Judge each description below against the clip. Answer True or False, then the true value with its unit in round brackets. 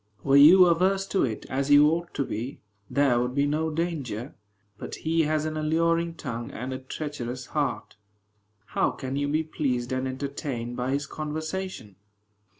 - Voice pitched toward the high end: False (145 Hz)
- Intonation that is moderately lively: True (3.6 semitones)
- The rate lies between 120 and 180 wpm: True (165 wpm)